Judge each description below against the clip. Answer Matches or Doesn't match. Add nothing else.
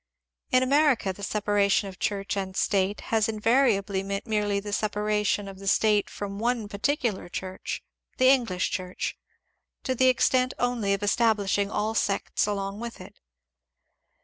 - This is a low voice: Doesn't match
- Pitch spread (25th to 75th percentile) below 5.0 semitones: Matches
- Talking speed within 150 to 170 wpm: Matches